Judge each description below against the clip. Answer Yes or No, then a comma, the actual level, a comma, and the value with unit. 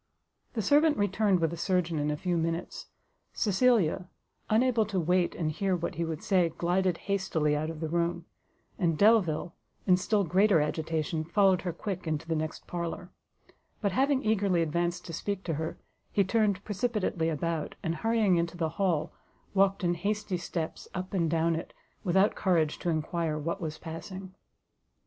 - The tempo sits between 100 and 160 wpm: No, average, 170 wpm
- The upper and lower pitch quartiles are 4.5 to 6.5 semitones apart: No, average, 3.3 semitones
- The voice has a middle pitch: Yes, medium, 175 Hz